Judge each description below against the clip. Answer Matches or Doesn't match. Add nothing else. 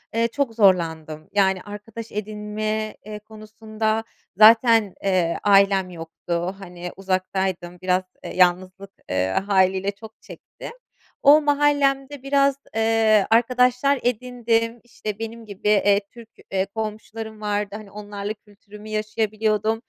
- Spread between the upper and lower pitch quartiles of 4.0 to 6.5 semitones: Doesn't match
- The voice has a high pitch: Matches